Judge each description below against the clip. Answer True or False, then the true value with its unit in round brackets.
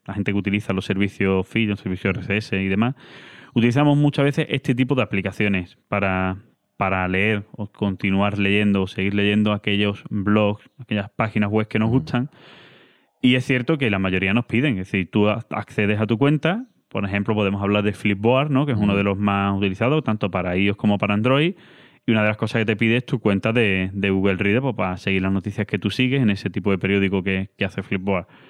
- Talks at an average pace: False (215 wpm)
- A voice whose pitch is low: True (105 Hz)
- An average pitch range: True (3.1 semitones)